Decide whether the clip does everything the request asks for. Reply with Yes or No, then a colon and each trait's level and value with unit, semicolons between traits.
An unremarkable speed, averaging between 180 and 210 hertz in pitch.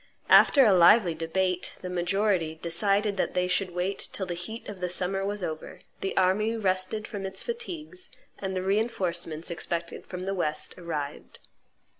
Yes: average, 160 wpm; medium, 185 Hz